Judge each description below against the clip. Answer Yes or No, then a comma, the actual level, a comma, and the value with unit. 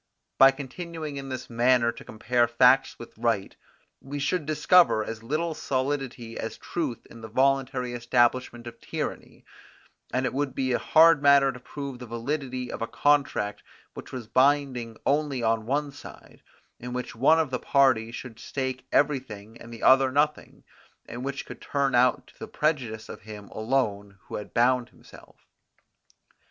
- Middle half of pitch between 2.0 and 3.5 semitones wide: Yes, average, 3.1 semitones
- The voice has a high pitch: No, low, 130 Hz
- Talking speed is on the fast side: No, average, 165 wpm